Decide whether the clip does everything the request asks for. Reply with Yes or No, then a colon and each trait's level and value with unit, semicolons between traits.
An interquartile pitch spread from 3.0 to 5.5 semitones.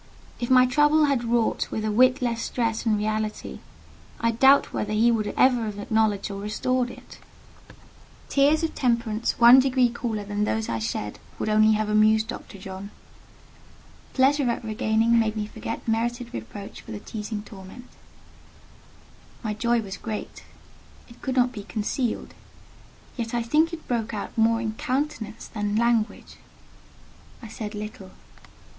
No: narrow, 2.4 semitones